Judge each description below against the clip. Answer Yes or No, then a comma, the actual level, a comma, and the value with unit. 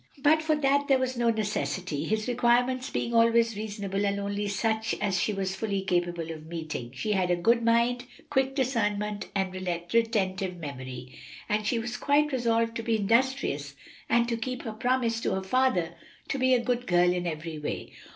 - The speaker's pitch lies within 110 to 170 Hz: No, high, 215 Hz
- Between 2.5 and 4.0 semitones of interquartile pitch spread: No, average, 4.8 semitones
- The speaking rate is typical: Yes, average, 185 wpm